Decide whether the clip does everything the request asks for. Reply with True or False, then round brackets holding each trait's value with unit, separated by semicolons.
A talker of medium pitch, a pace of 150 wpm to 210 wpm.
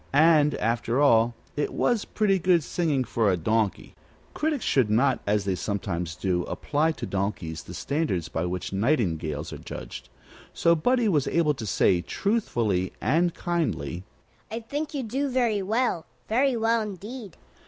True (145 Hz; 155 wpm)